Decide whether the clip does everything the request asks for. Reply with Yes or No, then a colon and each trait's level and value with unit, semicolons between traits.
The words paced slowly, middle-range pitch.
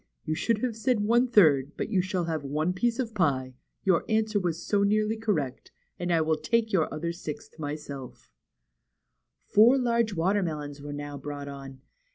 No: average, 175 wpm; medium, 175 Hz